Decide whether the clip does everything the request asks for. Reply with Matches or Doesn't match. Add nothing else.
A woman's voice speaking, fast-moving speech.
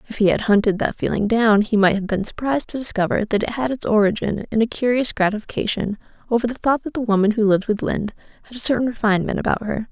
Matches